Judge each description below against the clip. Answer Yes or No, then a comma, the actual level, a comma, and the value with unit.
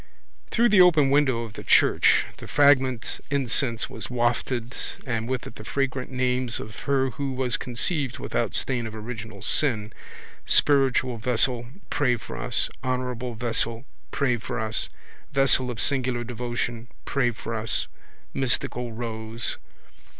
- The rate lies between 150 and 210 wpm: No, average, 140 wpm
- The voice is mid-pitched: No, low, 125 Hz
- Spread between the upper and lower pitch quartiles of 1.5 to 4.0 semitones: Yes, narrow, 2.5 semitones